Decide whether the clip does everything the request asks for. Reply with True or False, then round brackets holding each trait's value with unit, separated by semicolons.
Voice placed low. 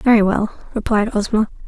False (215 Hz)